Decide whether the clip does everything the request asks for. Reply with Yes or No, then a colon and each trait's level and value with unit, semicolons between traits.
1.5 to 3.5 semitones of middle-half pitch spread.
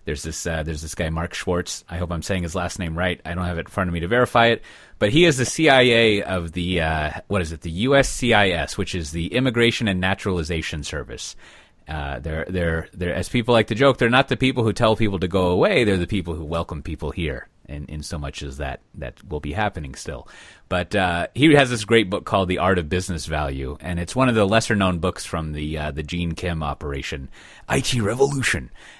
No: average, 5.1 semitones